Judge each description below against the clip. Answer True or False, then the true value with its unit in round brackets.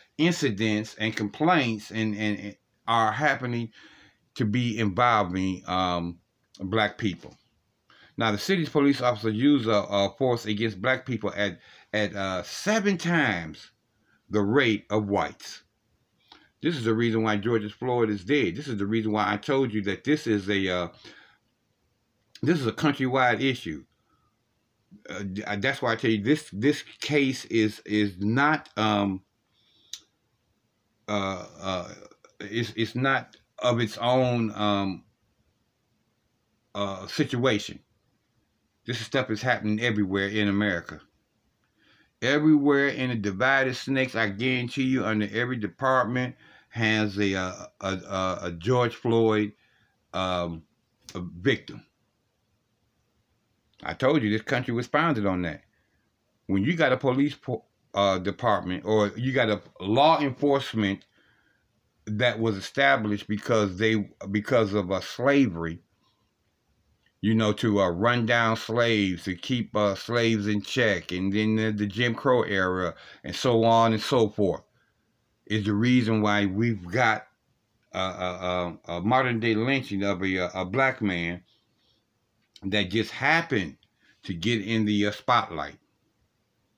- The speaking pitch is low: True (110 Hz)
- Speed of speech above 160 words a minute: False (140 wpm)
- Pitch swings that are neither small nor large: True (3.3 semitones)